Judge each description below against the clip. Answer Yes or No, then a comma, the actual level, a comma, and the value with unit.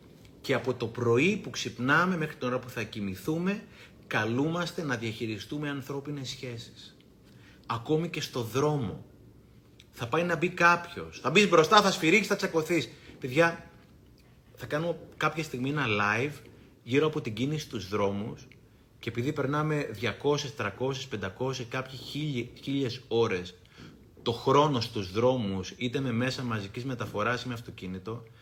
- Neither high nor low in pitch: No, low, 130 Hz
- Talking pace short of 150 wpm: Yes, average, 140 wpm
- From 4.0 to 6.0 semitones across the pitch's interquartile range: Yes, average, 4.4 semitones